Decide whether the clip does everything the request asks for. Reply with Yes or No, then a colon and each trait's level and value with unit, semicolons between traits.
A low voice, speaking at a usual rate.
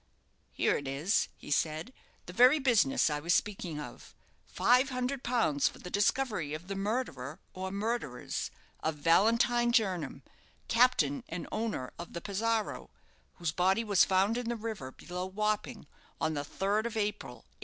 No: high, 200 Hz; average, 160 wpm